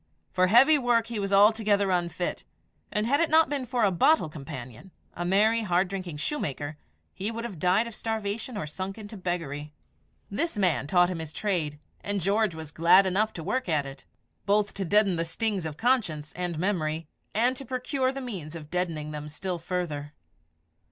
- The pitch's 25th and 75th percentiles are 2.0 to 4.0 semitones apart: No, wide, 5.4 semitones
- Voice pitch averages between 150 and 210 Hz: Yes, high, 190 Hz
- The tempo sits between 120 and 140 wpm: No, average, 185 wpm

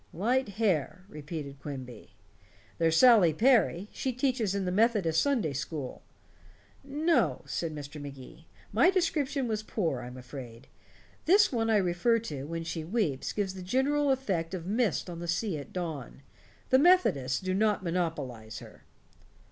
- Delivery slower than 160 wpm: Yes, average, 150 wpm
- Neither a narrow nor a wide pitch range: No, wide, 7.6 semitones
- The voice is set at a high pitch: No, medium, 180 Hz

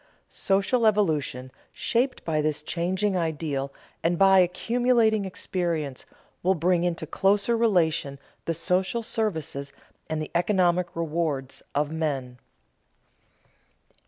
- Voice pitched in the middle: Yes, medium, 170 Hz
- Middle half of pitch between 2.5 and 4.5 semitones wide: Yes, average, 4.1 semitones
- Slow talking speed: Yes, slow, 105 wpm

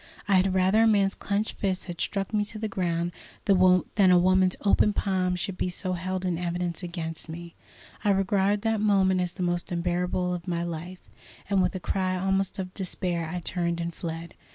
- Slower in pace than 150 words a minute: No, average, 200 wpm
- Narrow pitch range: Yes, narrow, 1.8 semitones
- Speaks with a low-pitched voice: No, medium, 185 Hz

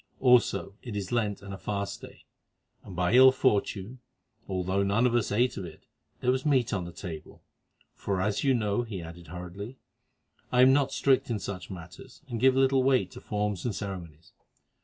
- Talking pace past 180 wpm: Yes, average, 190 wpm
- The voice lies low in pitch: Yes, low, 105 Hz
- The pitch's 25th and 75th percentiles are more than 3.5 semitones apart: Yes, average, 5.2 semitones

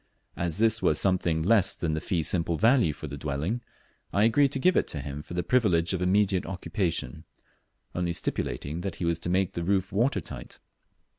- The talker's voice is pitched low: Yes, very low, 90 Hz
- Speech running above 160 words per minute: Yes, average, 195 wpm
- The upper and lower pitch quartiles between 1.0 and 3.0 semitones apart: No, average, 3.9 semitones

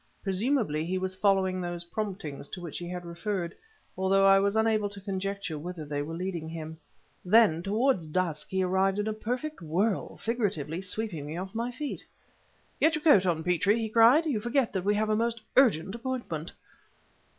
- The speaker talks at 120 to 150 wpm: No, average, 185 wpm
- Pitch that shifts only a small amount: No, average, 4.2 semitones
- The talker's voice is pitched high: Yes, high, 195 Hz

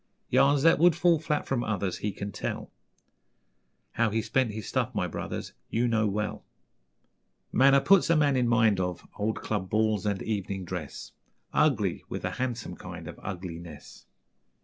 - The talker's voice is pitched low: Yes, low, 110 Hz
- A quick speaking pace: No, average, 165 wpm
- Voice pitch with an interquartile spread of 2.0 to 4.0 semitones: No, wide, 5.4 semitones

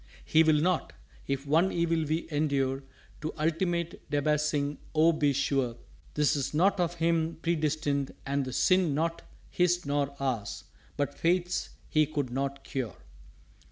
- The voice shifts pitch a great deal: No, average, 3.1 semitones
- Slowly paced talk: No, average, 145 wpm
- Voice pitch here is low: No, medium, 150 Hz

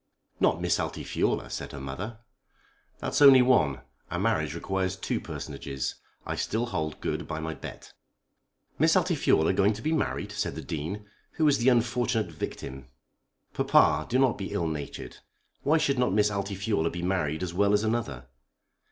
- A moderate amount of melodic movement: No, wide, 6.9 semitones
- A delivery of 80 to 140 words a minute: No, average, 165 wpm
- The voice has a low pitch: Yes, low, 100 Hz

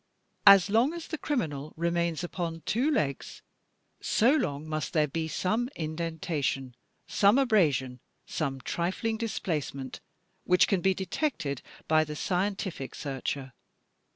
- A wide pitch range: Yes, wide, 5.7 semitones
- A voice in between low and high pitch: Yes, medium, 170 Hz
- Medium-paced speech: No, slow, 125 wpm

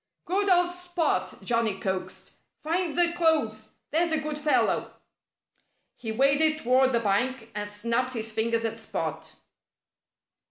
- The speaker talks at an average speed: No, slow, 130 wpm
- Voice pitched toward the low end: No, very high, 260 Hz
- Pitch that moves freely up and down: Yes, wide, 6.4 semitones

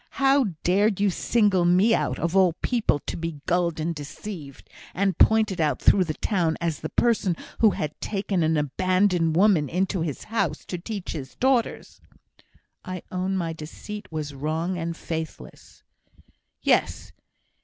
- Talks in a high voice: No, medium, 180 Hz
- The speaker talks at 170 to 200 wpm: No, average, 155 wpm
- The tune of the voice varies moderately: Yes, average, 4.0 semitones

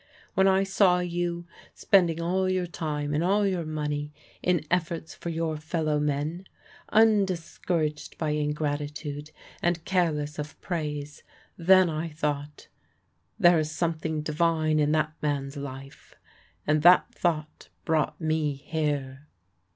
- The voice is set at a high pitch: No, medium, 155 Hz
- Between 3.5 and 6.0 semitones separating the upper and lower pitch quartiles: No, average, 2.7 semitones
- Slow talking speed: Yes, slow, 130 wpm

